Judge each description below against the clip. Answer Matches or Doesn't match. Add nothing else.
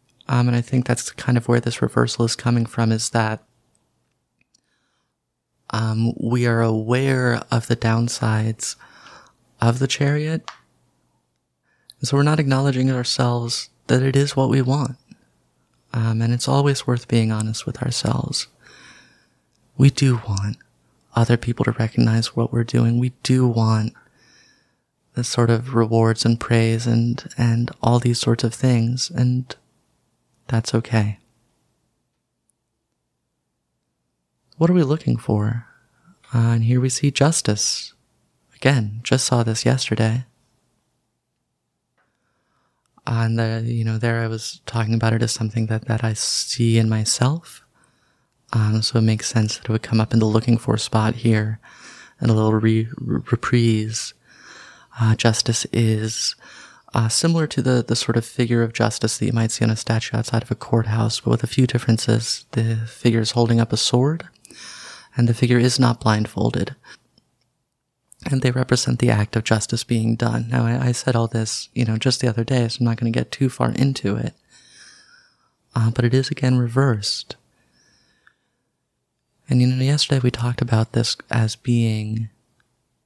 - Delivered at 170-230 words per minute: Doesn't match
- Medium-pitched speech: Doesn't match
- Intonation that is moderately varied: Doesn't match